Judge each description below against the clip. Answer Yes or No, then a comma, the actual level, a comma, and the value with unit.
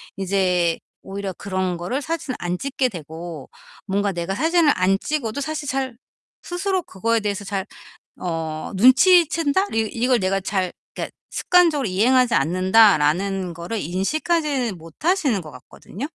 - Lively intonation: Yes, wide, 7.3 semitones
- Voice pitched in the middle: No, high, 200 Hz